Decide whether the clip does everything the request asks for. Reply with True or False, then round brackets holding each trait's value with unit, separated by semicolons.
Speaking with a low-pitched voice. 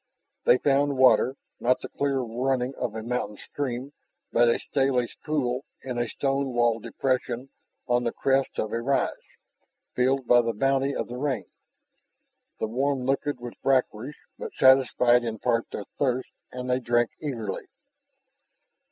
True (125 Hz)